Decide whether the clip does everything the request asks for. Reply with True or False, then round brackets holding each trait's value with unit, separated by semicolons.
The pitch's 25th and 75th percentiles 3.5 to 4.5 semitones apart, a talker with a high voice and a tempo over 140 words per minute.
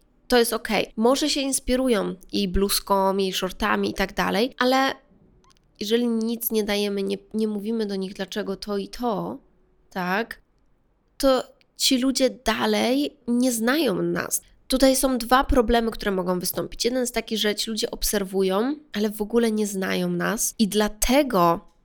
True (4.1 semitones; 215 Hz; 155 wpm)